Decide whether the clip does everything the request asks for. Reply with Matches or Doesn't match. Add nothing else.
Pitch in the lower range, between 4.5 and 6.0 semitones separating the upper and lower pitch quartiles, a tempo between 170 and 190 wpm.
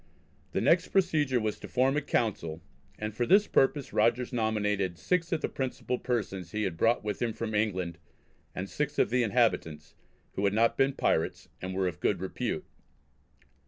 Matches